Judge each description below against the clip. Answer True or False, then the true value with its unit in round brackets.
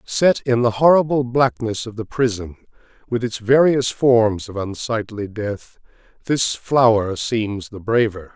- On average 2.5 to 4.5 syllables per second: True (4.0 syllables/s)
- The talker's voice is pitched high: False (115 Hz)